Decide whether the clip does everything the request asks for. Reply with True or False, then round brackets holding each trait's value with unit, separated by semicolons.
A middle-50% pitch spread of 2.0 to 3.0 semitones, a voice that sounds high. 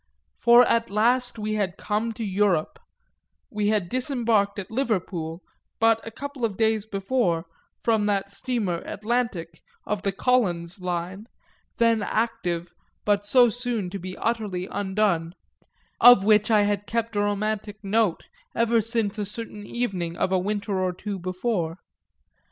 False (3.4 semitones; 210 Hz)